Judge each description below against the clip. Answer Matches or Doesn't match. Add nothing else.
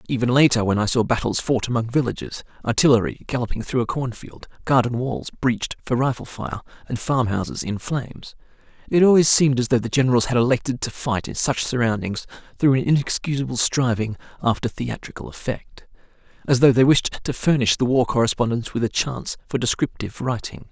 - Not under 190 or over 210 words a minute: Doesn't match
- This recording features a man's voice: Matches